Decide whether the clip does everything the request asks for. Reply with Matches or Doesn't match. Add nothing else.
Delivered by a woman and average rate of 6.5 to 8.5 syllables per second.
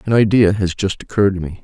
Doesn't match